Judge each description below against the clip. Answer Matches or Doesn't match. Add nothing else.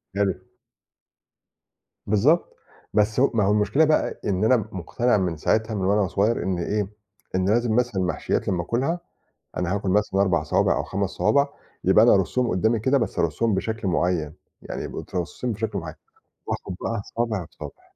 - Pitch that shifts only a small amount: Doesn't match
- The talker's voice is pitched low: Matches